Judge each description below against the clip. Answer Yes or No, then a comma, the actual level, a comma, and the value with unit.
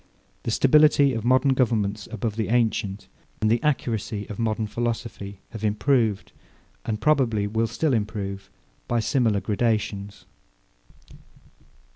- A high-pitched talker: No, low, 110 Hz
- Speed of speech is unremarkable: No, slow, 120 wpm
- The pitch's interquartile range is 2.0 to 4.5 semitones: Yes, average, 2.8 semitones